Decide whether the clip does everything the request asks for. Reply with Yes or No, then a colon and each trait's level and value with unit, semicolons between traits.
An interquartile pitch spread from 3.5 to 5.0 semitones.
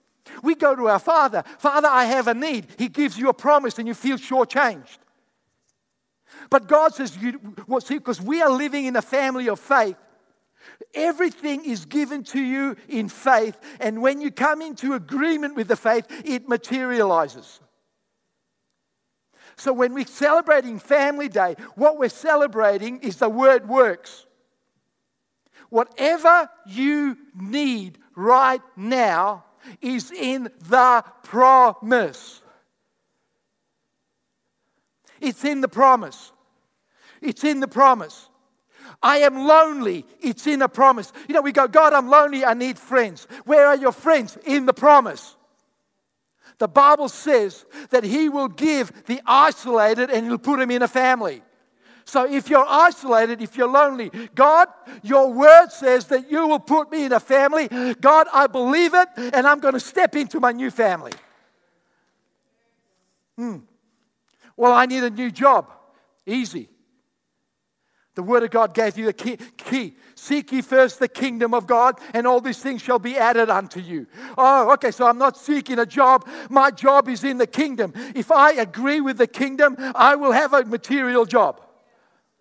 No: average, 3.1 semitones